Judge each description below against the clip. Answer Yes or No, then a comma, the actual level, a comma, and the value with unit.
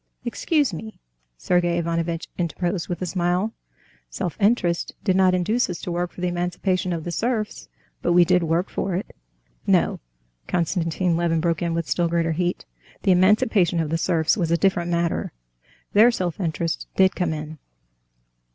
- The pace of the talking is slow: No, average, 170 wpm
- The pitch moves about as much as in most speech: No, narrow, 1.9 semitones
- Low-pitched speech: No, medium, 175 Hz